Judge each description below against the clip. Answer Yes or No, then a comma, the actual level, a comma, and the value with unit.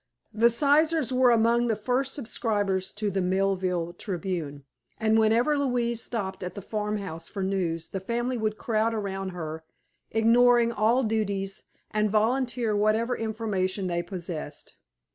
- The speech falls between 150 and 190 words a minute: No, average, 140 wpm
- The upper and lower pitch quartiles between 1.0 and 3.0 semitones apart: No, average, 3.7 semitones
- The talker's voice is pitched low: No, high, 215 Hz